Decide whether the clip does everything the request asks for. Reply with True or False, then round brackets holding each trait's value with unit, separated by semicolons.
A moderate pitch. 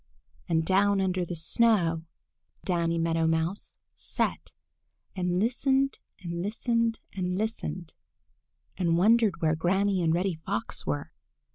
True (180 Hz)